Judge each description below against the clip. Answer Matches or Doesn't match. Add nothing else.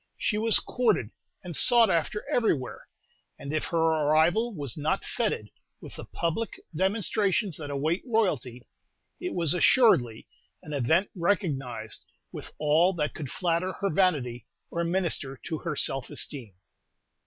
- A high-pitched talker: Doesn't match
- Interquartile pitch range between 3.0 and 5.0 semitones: Doesn't match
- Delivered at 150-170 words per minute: Doesn't match